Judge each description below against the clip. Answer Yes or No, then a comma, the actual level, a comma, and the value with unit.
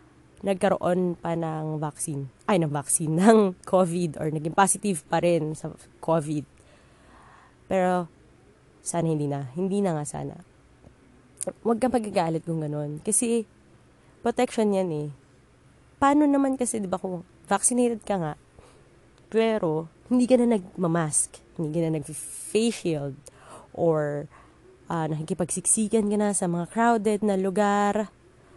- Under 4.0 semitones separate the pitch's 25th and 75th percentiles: No, average, 5.1 semitones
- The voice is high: No, medium, 175 Hz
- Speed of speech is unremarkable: Yes, average, 130 wpm